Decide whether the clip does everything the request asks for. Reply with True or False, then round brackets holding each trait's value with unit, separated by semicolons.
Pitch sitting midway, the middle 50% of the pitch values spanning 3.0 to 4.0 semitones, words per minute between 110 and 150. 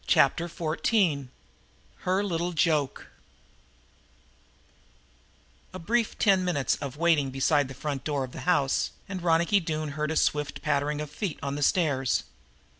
True (155 Hz; 3.7 semitones; 145 wpm)